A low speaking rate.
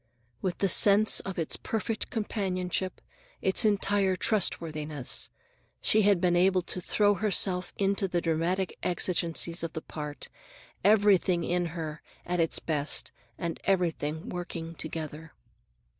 Yes: slow, 130 wpm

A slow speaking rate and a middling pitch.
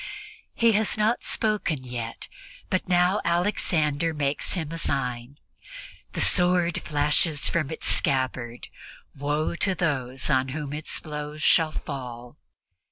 Yes: slow, 125 wpm; medium, 150 Hz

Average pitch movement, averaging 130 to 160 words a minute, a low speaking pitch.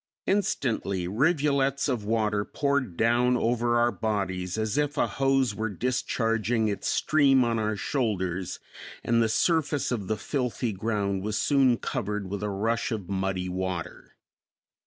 Yes: average, 4.4 semitones; average, 145 wpm; low, 115 Hz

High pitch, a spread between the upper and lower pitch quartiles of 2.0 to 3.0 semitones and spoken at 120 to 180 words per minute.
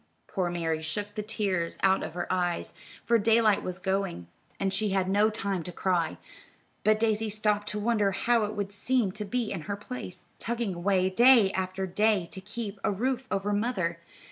No: high, 200 Hz; narrow, 2.6 semitones; average, 190 wpm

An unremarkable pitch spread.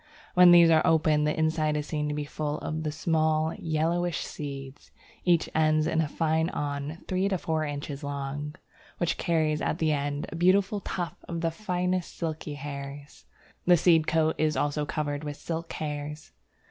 No: narrow, 2.0 semitones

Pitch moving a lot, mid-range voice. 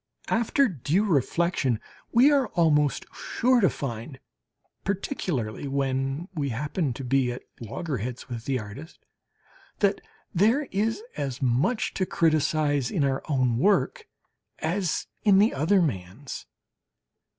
Yes: wide, 6.9 semitones; medium, 150 Hz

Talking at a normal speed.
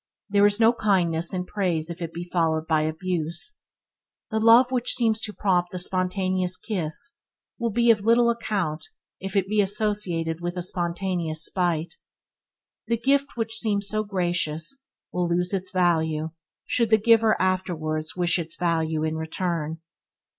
Yes: average, 155 wpm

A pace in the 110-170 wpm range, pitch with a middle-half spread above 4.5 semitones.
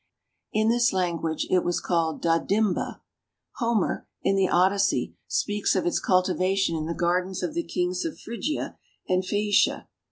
No: average, 150 wpm; average, 2.9 semitones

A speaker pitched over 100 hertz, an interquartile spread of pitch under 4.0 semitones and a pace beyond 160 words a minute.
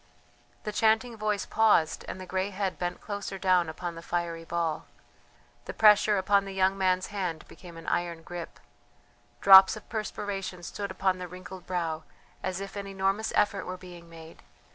Yes: medium, 185 Hz; narrow, 2.5 semitones; average, 170 wpm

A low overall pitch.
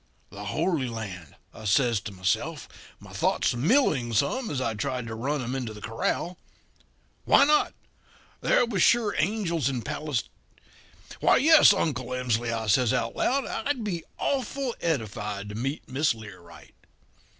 Yes: low, 125 Hz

